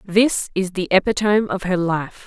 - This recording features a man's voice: No, female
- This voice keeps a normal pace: Yes, average, 185 wpm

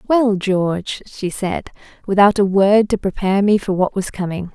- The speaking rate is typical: Yes, average, 185 wpm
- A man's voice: No, female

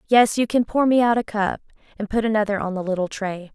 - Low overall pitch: No, high, 210 Hz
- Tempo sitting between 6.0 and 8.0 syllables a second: Yes, 6.1 syllables/s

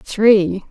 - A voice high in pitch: Yes, high, 200 Hz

